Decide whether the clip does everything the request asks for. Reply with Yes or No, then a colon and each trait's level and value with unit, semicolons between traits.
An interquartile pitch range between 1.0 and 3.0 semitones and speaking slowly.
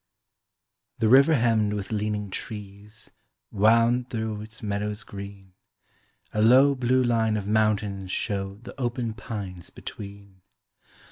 Yes: narrow, 2.4 semitones; slow, 120 wpm